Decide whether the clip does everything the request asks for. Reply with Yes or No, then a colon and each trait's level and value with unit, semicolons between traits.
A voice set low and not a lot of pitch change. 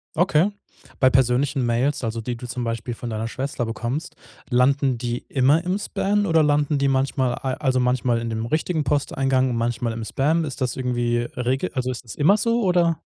No: low, 130 Hz; average, 3.5 semitones